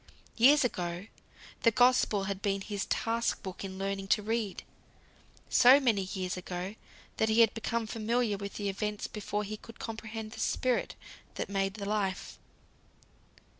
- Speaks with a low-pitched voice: No, high, 210 Hz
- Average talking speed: Yes, average, 155 wpm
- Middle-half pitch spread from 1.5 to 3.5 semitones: Yes, average, 2.7 semitones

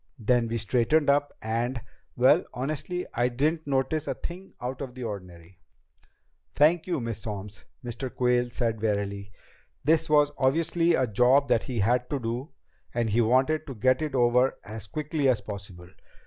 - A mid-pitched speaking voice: No, low, 125 Hz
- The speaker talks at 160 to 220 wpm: Yes, average, 165 wpm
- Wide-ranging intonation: No, average, 4.3 semitones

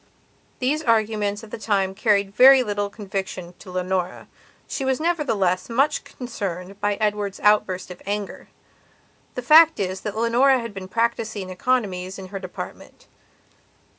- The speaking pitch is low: No, high, 205 Hz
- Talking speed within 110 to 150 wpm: Yes, average, 140 wpm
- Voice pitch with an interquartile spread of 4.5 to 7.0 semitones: No, average, 3.7 semitones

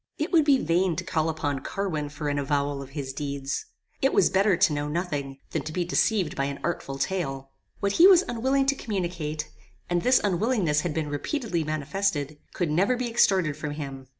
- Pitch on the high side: No, medium, 160 Hz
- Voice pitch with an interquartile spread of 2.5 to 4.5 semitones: No, wide, 5.5 semitones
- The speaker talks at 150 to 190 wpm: No, average, 200 wpm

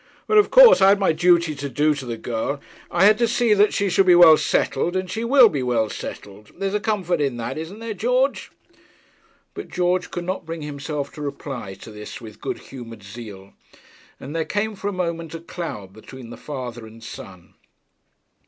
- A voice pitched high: No, medium, 160 Hz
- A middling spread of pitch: No, wide, 8.2 semitones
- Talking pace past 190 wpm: Yes, fast, 205 wpm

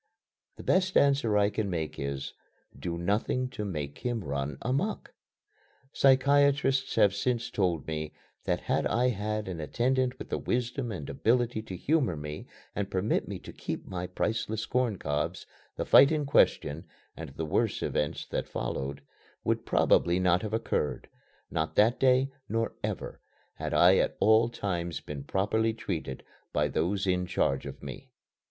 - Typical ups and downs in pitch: No, wide, 7.0 semitones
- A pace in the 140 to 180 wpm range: Yes, average, 160 wpm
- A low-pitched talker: Yes, low, 105 Hz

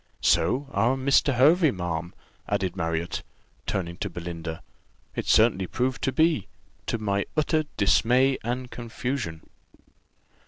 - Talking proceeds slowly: Yes, slow, 120 wpm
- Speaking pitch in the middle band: No, low, 115 Hz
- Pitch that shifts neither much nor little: No, wide, 7.1 semitones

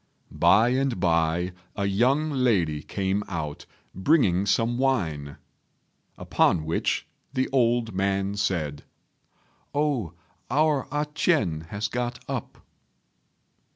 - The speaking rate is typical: No, slow, 105 wpm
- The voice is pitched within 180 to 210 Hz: No, low, 100 Hz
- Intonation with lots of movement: Yes, wide, 6.8 semitones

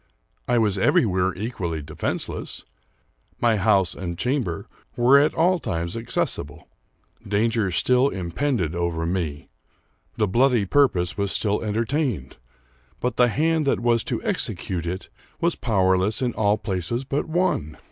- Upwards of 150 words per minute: No, slow, 135 wpm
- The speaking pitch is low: Yes, low, 105 Hz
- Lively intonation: Yes, wide, 5.7 semitones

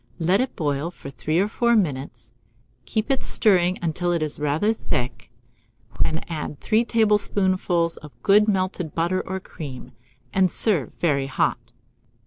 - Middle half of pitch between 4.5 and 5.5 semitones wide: Yes, average, 5.1 semitones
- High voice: No, medium, 175 Hz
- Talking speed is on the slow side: No, average, 145 wpm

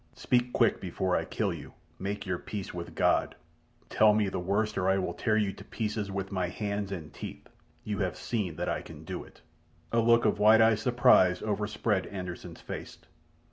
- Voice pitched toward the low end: Yes, low, 100 Hz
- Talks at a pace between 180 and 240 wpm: Yes, average, 195 wpm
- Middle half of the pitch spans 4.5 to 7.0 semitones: No, average, 2.7 semitones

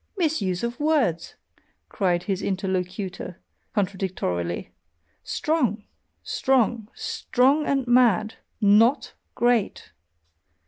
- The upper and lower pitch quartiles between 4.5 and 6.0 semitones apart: Yes, average, 5.1 semitones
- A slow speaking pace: Yes, slow, 80 wpm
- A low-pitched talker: No, high, 215 Hz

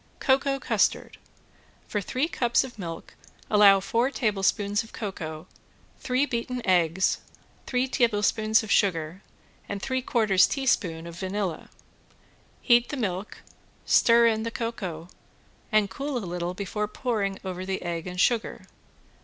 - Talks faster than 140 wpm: No, slow, 135 wpm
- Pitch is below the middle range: No, high, 210 Hz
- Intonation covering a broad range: No, average, 4.5 semitones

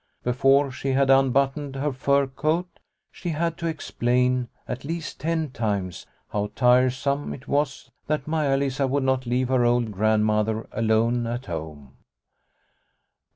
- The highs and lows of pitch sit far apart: No, average, 3.0 semitones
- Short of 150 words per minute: Yes, average, 140 wpm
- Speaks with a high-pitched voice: No, low, 130 Hz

